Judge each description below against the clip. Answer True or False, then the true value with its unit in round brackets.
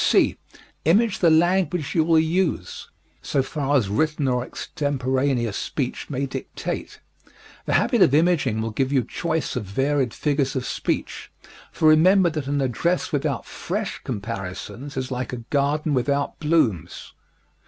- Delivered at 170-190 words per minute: False (145 wpm)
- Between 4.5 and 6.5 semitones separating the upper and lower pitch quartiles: False (3.9 semitones)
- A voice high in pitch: False (140 Hz)